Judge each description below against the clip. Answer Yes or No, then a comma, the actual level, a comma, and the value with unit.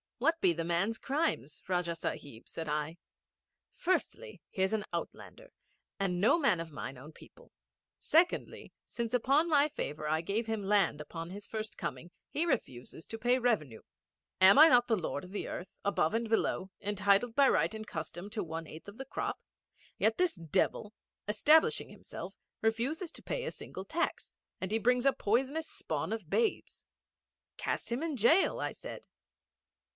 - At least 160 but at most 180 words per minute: Yes, average, 170 wpm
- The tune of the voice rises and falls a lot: Yes, wide, 7.5 semitones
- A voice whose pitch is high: Yes, high, 215 Hz